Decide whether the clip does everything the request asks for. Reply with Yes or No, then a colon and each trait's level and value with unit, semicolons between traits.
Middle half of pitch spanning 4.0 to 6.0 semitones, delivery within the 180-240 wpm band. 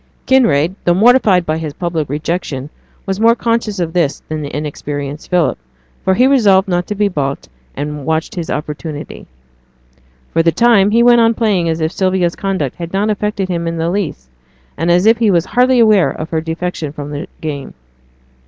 Yes: average, 5.0 semitones; average, 185 wpm